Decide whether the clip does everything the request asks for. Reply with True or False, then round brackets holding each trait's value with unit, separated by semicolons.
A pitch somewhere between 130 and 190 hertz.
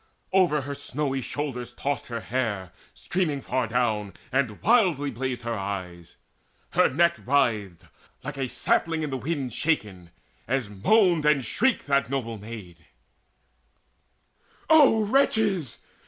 True (135 Hz)